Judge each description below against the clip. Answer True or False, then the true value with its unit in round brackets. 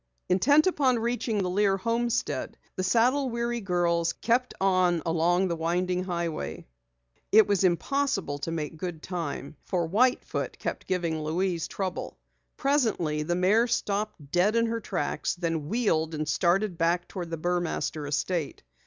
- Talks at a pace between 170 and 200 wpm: False (150 wpm)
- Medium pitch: True (180 Hz)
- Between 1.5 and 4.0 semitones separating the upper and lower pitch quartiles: False (5.2 semitones)